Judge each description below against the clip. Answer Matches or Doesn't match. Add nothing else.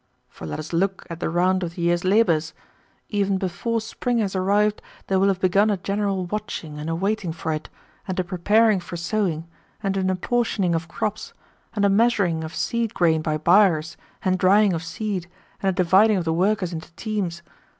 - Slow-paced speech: Doesn't match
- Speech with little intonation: Doesn't match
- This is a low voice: Doesn't match